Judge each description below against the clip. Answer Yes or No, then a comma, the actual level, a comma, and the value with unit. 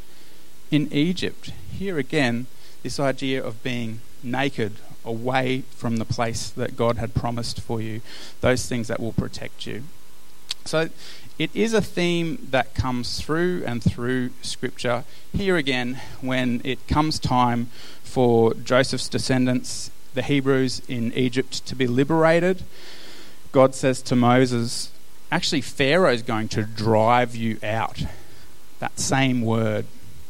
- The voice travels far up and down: No, average, 2.7 semitones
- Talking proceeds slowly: Yes, slow, 130 wpm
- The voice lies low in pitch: Yes, low, 125 Hz